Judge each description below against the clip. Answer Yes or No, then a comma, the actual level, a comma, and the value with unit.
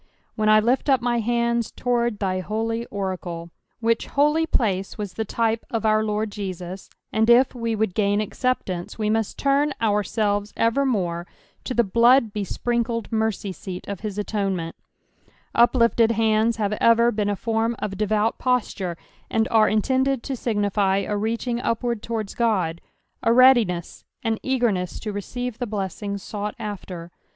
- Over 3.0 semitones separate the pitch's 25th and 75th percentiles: No, average, 2.7 semitones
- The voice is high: Yes, high, 220 Hz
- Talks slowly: No, average, 160 wpm